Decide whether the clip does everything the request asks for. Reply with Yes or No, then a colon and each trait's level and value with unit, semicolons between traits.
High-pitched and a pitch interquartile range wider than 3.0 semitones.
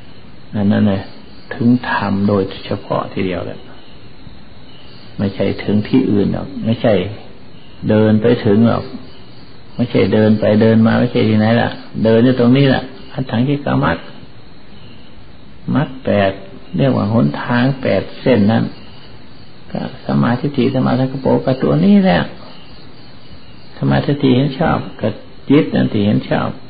No: low, 115 Hz; average, 3.7 semitones